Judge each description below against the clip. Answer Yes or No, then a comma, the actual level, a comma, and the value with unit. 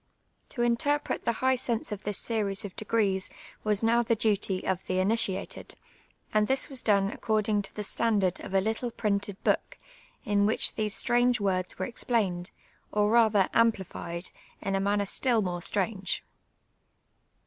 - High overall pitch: Yes, high, 210 Hz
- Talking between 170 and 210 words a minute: No, average, 160 wpm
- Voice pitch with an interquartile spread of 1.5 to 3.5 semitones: Yes, average, 2.9 semitones